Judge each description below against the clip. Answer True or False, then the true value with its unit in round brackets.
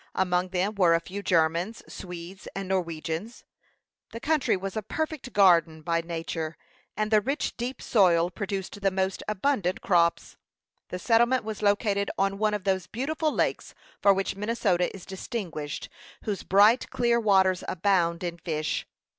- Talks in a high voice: True (195 Hz)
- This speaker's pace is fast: False (155 wpm)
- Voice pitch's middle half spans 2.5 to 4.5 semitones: True (3.6 semitones)